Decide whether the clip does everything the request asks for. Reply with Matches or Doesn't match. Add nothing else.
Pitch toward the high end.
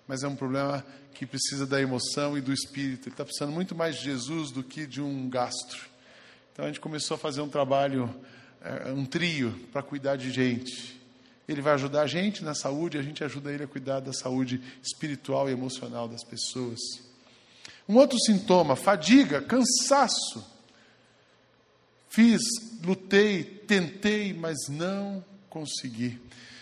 Doesn't match